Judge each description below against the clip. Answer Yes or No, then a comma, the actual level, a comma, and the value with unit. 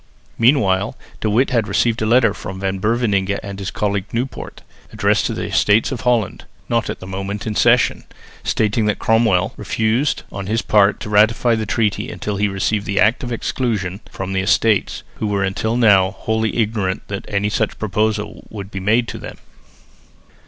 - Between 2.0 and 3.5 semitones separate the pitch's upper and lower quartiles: Yes, narrow, 2.4 semitones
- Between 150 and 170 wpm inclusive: No, average, 180 wpm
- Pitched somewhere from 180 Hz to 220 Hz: No, low, 105 Hz